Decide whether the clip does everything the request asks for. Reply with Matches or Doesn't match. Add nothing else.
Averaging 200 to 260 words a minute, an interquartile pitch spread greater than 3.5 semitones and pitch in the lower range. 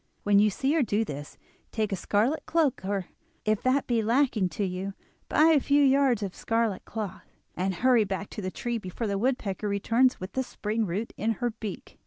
Doesn't match